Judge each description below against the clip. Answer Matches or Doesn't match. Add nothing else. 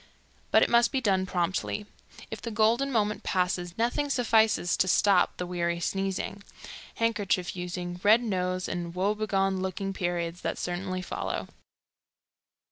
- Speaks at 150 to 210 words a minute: Doesn't match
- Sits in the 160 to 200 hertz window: Matches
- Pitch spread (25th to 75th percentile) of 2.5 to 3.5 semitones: Matches